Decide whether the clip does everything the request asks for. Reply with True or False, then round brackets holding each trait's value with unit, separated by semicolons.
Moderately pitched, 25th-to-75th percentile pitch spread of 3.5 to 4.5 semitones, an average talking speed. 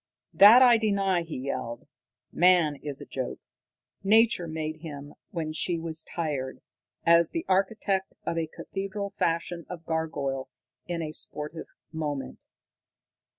False (165 Hz; 3.9 semitones; 130 wpm)